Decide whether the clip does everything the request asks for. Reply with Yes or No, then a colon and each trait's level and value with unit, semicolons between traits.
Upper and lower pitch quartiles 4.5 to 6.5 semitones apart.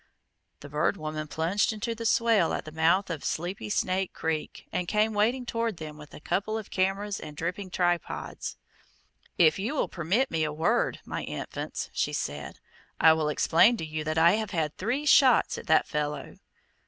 Yes: wide, 5.4 semitones